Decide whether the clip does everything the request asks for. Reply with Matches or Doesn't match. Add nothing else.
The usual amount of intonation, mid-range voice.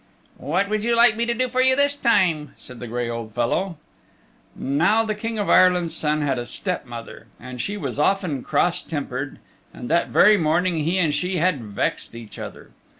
Doesn't match